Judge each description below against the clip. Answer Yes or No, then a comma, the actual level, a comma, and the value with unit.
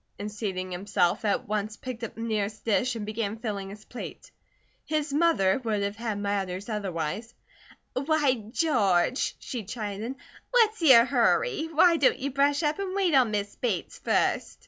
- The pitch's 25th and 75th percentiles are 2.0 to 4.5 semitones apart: No, wide, 5.5 semitones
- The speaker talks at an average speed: Yes, average, 165 wpm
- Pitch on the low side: No, high, 225 Hz